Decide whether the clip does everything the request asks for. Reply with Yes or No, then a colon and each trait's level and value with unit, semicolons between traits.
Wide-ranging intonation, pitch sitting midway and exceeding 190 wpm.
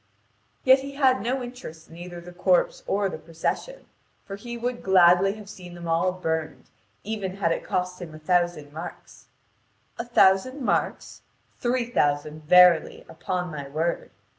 No: wide, 6.3 semitones; medium, 180 Hz; average, 160 wpm